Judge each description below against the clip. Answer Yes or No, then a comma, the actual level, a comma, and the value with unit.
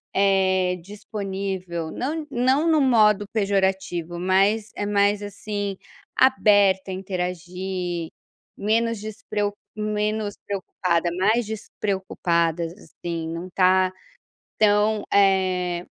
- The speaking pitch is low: No, high, 195 Hz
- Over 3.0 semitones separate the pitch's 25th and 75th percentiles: No, narrow, 2.5 semitones